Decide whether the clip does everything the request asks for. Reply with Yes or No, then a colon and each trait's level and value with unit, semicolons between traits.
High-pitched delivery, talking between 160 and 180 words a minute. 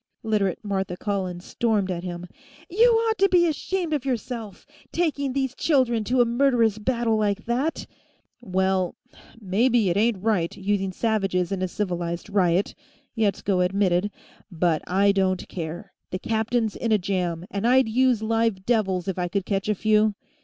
Yes: high, 210 Hz; average, 165 wpm